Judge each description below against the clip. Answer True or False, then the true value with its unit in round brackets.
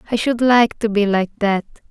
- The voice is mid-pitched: False (220 Hz)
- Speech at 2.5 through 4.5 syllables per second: False (4.8 syllables/s)